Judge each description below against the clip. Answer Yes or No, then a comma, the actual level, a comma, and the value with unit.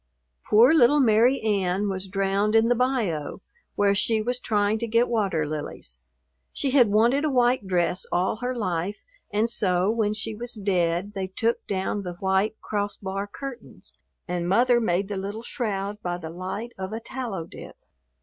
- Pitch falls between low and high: No, high, 205 Hz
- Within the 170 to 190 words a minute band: Yes, average, 175 wpm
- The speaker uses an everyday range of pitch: Yes, average, 3.6 semitones